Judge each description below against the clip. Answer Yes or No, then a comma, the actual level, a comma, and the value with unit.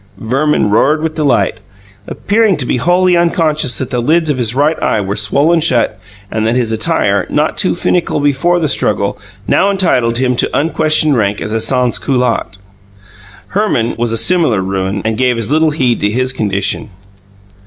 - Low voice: Yes, low, 130 Hz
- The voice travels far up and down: Yes, wide, 5.9 semitones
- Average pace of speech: Yes, average, 175 wpm